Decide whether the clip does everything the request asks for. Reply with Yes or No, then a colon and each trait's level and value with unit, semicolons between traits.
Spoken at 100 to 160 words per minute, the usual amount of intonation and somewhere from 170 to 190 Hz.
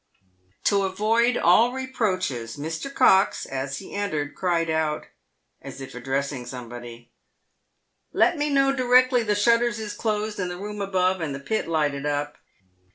No: average, 155 wpm; wide, 7.6 semitones; medium, 185 Hz